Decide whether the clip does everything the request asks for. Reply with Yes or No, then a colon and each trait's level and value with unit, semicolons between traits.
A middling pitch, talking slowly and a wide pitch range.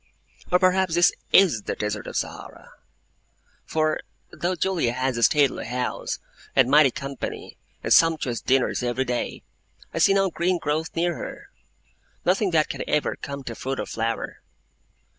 No: medium, 150 Hz; average, 155 wpm; wide, 5.7 semitones